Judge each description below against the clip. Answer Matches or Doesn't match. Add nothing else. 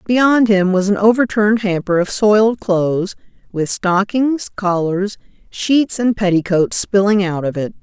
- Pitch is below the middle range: Doesn't match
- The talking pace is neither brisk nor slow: Matches